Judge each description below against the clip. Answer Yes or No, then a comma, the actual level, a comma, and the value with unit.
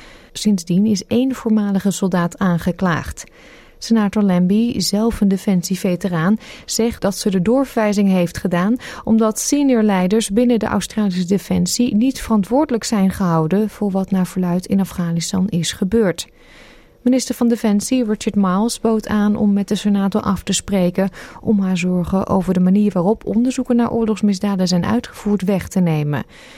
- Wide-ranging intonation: No, average, 3.1 semitones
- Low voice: No, high, 205 Hz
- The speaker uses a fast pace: No, average, 150 wpm